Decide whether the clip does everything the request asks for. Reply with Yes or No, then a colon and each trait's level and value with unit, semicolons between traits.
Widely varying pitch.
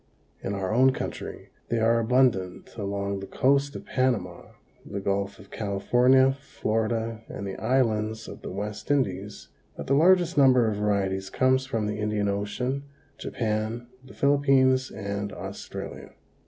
No: average, 4.5 semitones